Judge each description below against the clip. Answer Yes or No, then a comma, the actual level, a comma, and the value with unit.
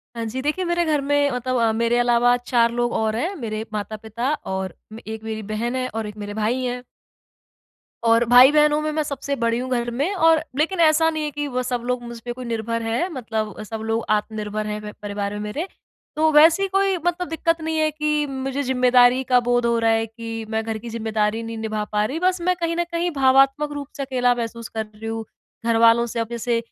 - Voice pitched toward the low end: No, high, 245 Hz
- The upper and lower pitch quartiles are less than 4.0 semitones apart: No, average, 4.7 semitones